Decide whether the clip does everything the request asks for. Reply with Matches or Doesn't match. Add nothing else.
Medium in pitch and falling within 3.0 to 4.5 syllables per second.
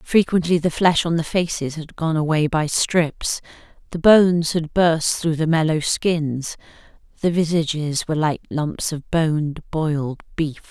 Matches